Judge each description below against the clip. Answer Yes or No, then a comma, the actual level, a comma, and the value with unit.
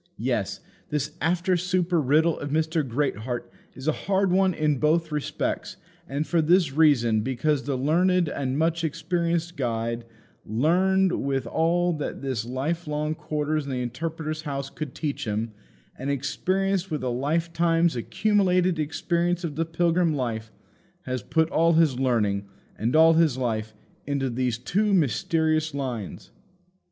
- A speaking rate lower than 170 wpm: Yes, average, 145 wpm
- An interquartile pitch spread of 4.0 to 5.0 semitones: Yes, average, 4.4 semitones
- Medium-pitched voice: Yes, medium, 155 Hz